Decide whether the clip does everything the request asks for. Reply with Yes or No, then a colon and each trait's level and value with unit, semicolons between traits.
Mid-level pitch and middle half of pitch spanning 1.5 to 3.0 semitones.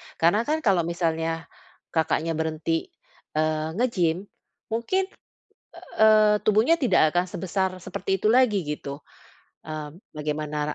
No: medium, 175 Hz; average, 5.3 semitones